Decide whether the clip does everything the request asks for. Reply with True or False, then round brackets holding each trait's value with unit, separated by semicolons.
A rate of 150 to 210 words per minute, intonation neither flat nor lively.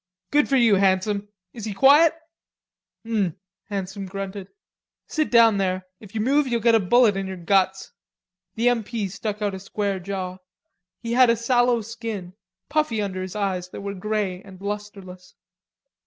True (170 wpm; 3.4 semitones)